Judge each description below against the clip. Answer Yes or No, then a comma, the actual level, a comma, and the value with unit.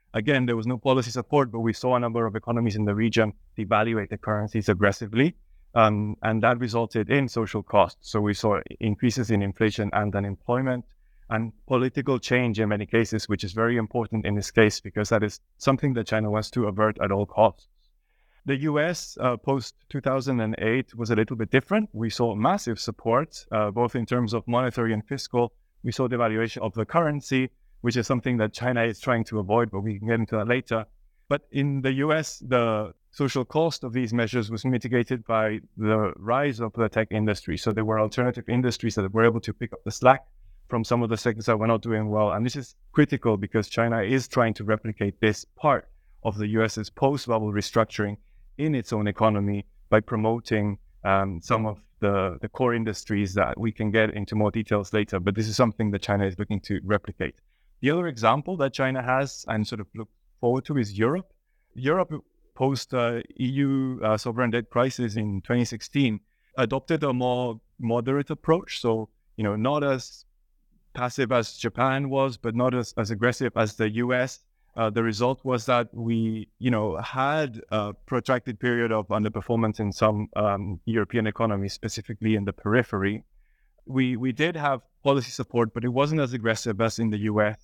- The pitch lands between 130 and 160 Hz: No, low, 115 Hz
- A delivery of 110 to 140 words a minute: No, average, 190 wpm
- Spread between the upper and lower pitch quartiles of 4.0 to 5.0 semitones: No, average, 2.8 semitones